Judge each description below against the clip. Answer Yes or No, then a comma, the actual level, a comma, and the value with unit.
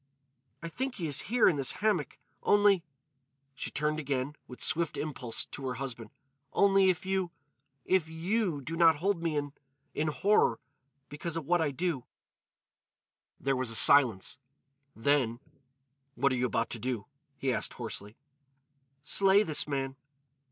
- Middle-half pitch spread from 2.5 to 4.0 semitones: No, average, 4.7 semitones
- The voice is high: No, medium, 145 Hz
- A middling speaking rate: Yes, average, 145 wpm